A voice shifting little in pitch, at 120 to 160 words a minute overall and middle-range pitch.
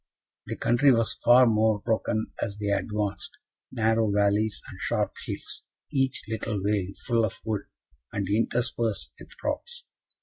No: narrow, 2.2 semitones; average, 140 wpm; low, 110 Hz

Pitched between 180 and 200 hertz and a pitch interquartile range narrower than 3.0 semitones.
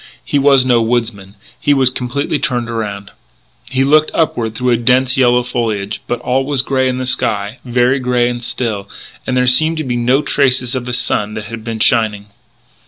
No: low, 125 Hz; narrow, 2.4 semitones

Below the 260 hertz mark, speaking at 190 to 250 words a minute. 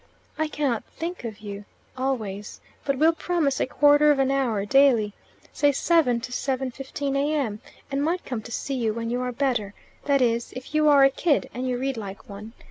No: very high, 265 Hz; average, 195 wpm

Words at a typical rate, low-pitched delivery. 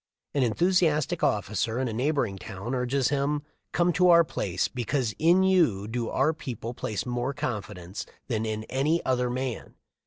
Yes: average, 160 wpm; low, 125 Hz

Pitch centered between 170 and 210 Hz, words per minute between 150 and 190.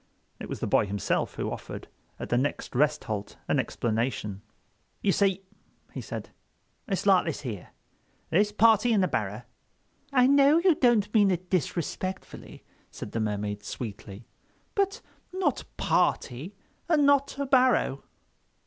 No: medium, 185 Hz; average, 140 wpm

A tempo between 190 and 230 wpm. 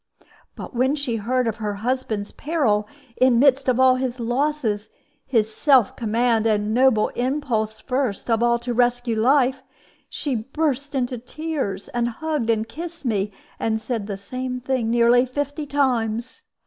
No: average, 160 wpm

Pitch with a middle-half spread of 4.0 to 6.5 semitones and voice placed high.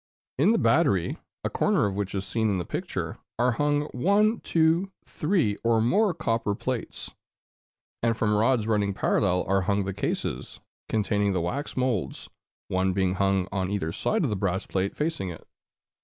No: wide, 5.5 semitones; low, 105 Hz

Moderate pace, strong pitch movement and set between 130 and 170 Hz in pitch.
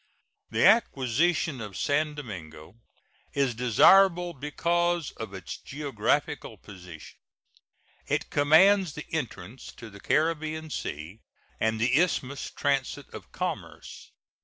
No: slow, 110 wpm; wide, 6.3 semitones; medium, 140 Hz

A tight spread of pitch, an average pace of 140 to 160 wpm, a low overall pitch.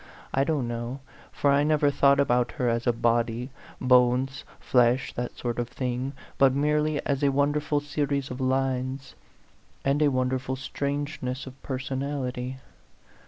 Yes: narrow, 2.2 semitones; average, 145 wpm; low, 130 Hz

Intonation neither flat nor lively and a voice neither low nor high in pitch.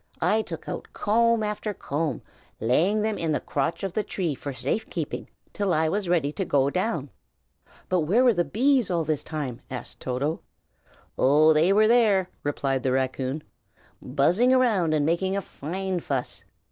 No: wide, 6.3 semitones; medium, 170 Hz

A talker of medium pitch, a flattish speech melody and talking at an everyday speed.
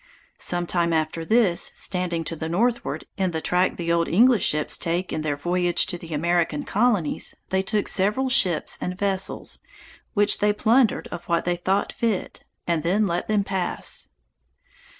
No: medium, 180 Hz; average, 3.3 semitones; average, 165 wpm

